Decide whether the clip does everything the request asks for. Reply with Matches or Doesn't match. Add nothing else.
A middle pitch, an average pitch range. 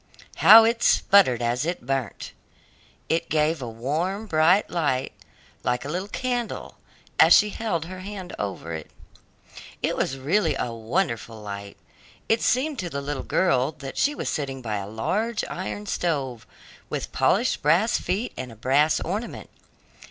Doesn't match